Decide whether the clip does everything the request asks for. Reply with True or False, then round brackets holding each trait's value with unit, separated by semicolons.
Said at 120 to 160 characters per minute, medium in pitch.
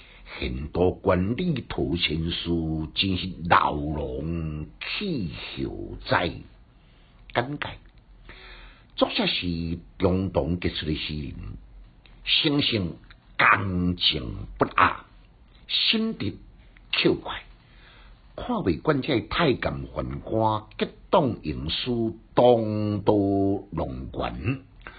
False (125 characters per minute; 90 Hz)